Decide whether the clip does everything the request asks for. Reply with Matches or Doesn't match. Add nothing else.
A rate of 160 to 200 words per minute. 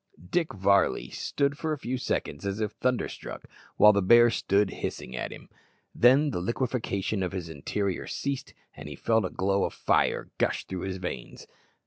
Matches